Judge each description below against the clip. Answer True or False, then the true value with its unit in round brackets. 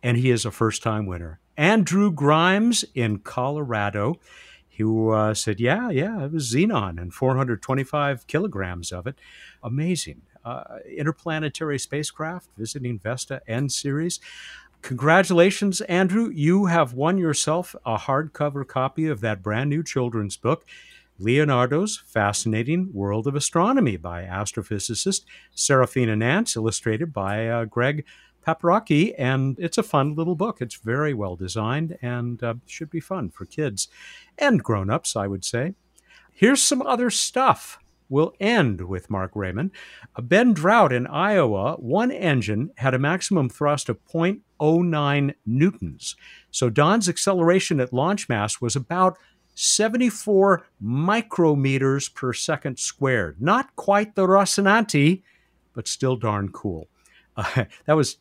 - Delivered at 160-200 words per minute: False (135 wpm)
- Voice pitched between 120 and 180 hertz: True (140 Hz)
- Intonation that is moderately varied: False (7.3 semitones)